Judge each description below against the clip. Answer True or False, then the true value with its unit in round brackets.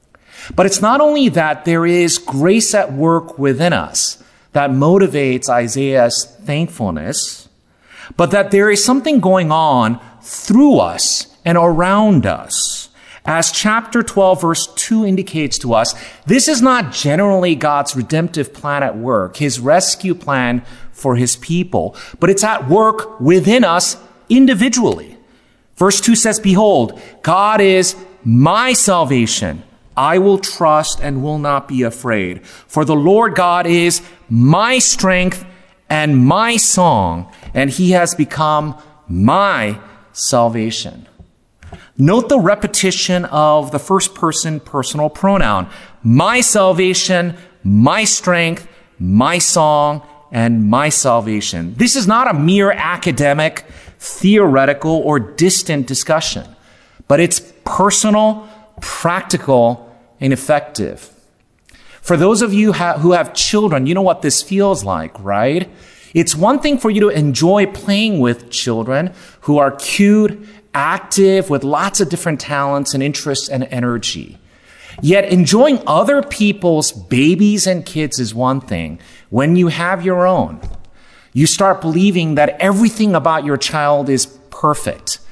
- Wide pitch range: True (6.2 semitones)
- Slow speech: True (130 wpm)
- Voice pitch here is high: False (165 Hz)